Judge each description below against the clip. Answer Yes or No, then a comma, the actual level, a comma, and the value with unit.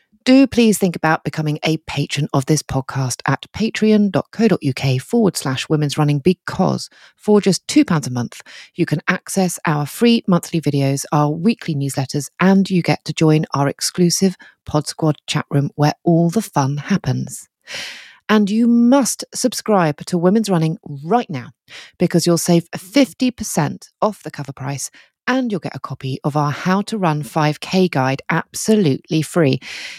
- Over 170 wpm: No, average, 160 wpm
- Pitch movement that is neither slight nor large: No, wide, 5.8 semitones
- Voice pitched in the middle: Yes, medium, 165 Hz